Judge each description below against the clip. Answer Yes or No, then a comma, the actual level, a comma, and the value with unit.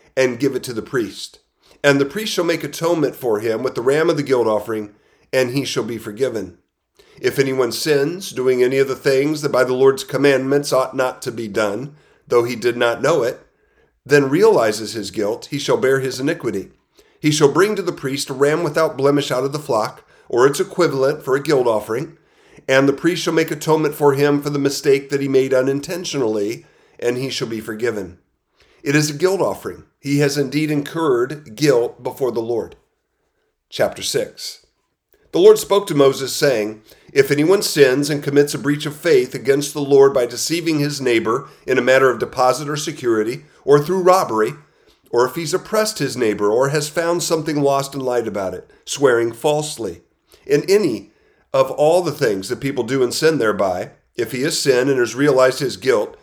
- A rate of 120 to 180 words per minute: No, average, 195 wpm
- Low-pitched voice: No, medium, 145 Hz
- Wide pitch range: No, average, 4.3 semitones